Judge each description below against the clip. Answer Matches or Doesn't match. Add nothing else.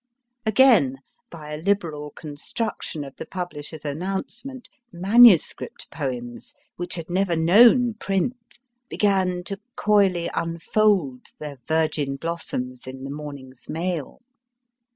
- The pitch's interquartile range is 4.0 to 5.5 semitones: Matches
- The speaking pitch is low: Doesn't match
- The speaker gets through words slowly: Matches